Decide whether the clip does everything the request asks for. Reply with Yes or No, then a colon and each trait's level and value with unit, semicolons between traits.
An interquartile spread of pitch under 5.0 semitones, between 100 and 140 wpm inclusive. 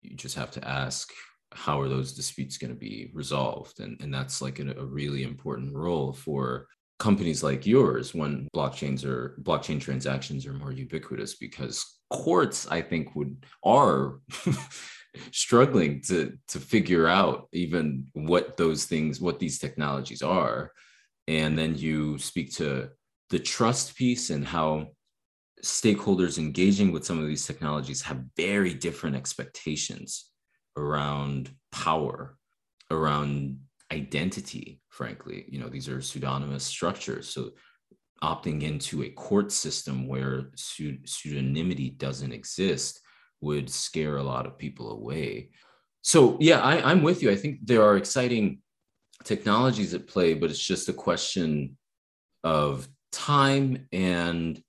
Yes: average, 3.7 semitones; slow, 135 wpm